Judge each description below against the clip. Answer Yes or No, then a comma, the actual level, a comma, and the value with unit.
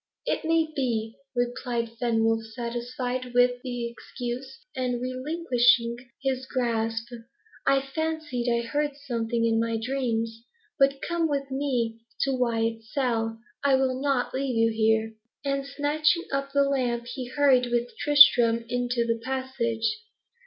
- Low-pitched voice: No, high, 245 Hz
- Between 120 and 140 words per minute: Yes, slow, 135 wpm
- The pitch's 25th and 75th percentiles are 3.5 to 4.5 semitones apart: No, average, 2.8 semitones